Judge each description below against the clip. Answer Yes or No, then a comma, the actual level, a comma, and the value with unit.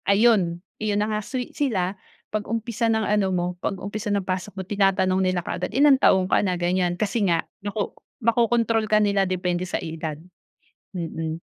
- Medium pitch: No, high, 195 Hz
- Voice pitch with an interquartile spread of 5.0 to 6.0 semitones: No, average, 2.9 semitones